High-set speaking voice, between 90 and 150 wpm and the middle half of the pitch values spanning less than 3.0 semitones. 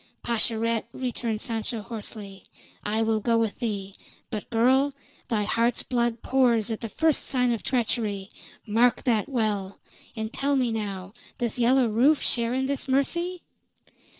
Yes: high, 230 Hz; average, 145 wpm; narrow, 2.6 semitones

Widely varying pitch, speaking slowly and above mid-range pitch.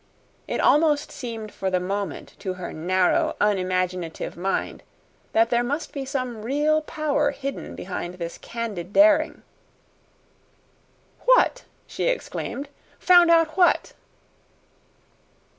Yes: wide, 8.3 semitones; slow, 110 wpm; high, 235 Hz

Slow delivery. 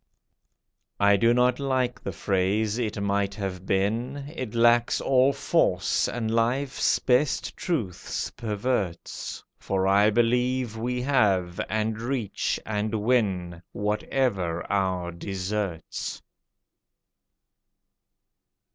Yes: slow, 100 wpm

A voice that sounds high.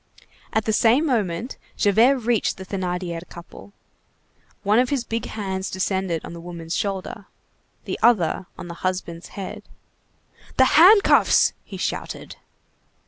Yes: high, 195 Hz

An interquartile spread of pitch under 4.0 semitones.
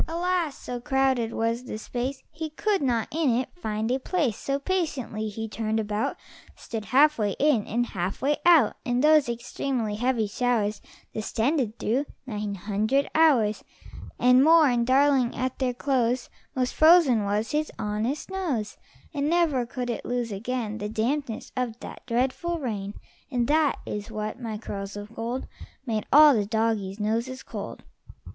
No: average, 4.3 semitones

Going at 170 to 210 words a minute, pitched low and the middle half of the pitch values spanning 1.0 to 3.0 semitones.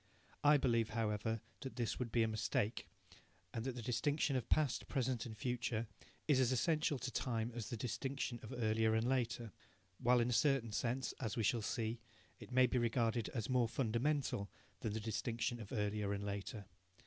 Yes: average, 185 wpm; low, 120 Hz; narrow, 2.5 semitones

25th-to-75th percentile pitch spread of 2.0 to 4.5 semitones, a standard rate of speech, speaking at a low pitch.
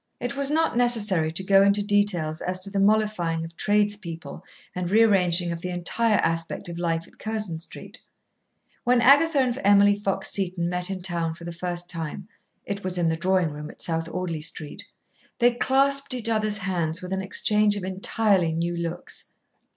No: average, 3.8 semitones; average, 180 wpm; medium, 185 Hz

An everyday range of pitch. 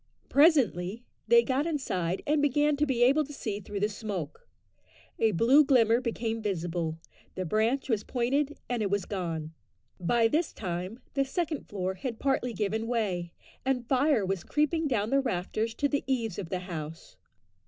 No: wide, 6.3 semitones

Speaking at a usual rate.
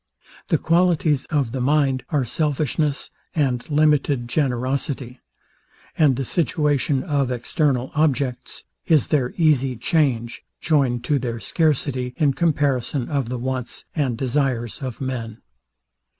No: slow, 120 wpm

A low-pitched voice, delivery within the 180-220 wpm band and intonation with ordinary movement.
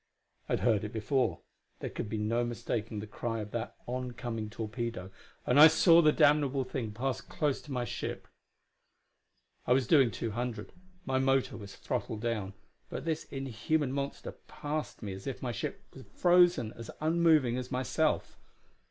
No: low, 125 Hz; average, 170 wpm; average, 3.9 semitones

